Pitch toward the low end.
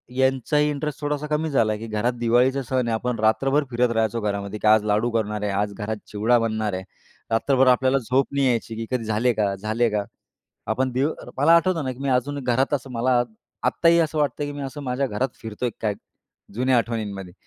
Yes: low, 125 Hz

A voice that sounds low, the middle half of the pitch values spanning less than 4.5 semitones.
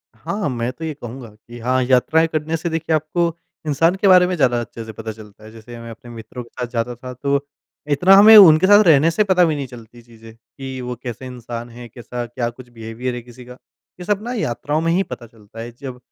No: low, 125 Hz; average, 5.3 semitones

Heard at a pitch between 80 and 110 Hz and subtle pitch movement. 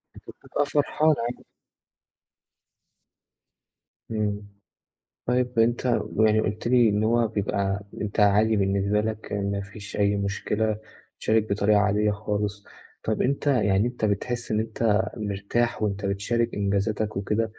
Yes: low, 105 Hz; narrow, 2.1 semitones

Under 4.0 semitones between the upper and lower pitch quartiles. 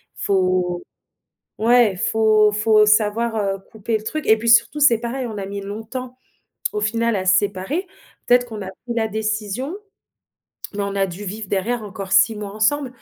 Yes: average, 2.7 semitones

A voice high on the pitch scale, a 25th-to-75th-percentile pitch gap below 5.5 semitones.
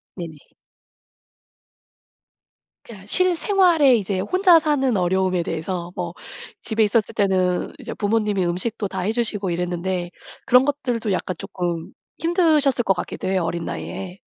No: high, 200 Hz; wide, 6.1 semitones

